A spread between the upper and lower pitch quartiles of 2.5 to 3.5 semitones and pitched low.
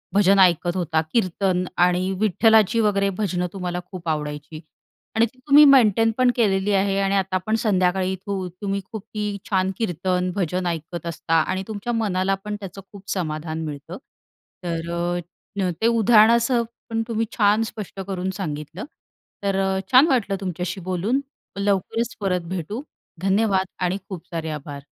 No: average, 3.2 semitones; high, 190 Hz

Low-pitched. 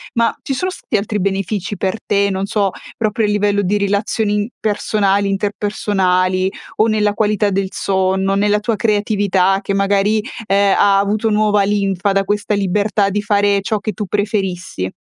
No: high, 205 Hz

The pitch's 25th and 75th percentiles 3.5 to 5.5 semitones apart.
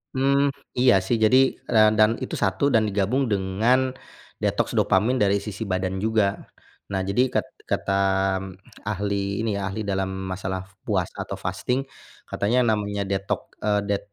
No: narrow, 2.5 semitones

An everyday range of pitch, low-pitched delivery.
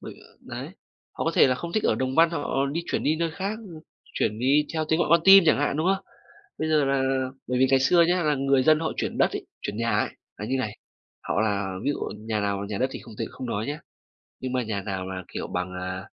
No: wide, 6.6 semitones; low, 130 Hz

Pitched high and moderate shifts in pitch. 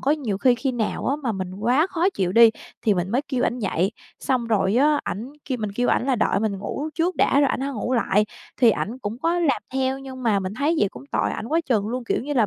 Yes: high, 245 Hz; average, 4.7 semitones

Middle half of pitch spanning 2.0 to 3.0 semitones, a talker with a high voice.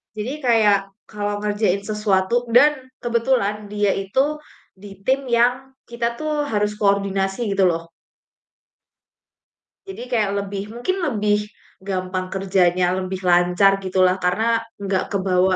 No: average, 3.6 semitones; high, 205 Hz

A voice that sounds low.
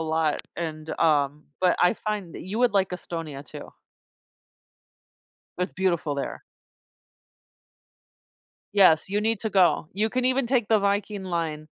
No: medium, 185 Hz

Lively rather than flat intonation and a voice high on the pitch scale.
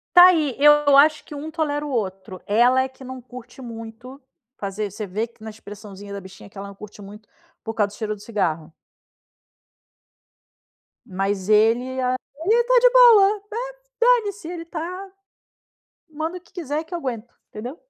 Yes: wide, 7.5 semitones; very high, 255 Hz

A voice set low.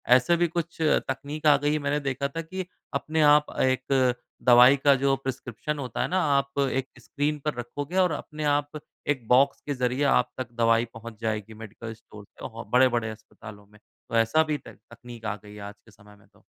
Yes: low, 130 Hz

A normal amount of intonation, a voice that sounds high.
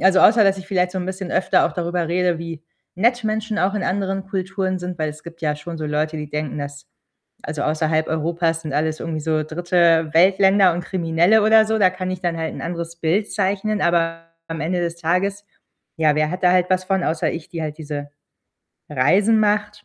No: average, 3.2 semitones; medium, 175 Hz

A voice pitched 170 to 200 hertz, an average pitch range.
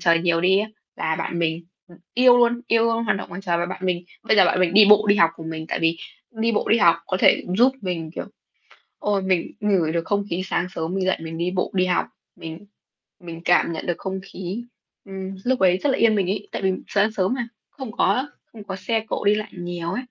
Yes: high, 190 Hz; average, 3.6 semitones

